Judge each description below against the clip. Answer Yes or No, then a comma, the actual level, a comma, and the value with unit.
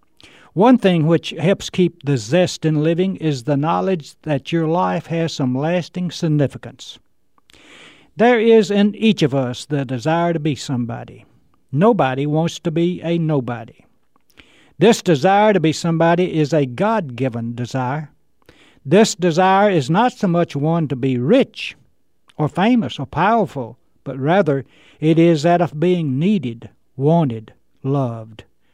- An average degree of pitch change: Yes, average, 4.8 semitones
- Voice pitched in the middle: Yes, medium, 160 Hz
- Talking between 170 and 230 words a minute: No, average, 145 wpm